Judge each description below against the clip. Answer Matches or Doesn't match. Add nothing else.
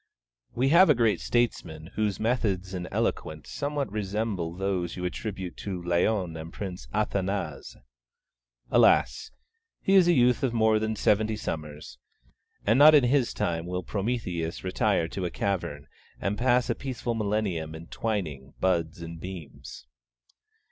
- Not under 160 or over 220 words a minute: Doesn't match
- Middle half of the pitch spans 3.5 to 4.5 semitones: Doesn't match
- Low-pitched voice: Matches